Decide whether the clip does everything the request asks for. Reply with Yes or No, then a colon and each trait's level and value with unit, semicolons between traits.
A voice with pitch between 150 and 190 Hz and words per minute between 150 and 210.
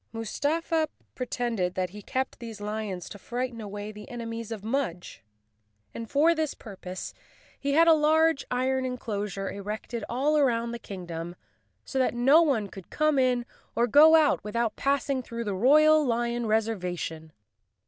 No: high, 235 Hz; average, 160 wpm